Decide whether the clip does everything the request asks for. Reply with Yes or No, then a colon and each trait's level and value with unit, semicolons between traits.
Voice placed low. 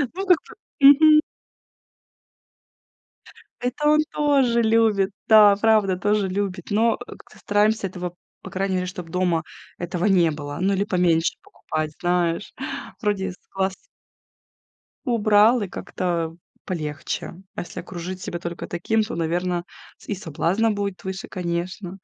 No: high, 190 Hz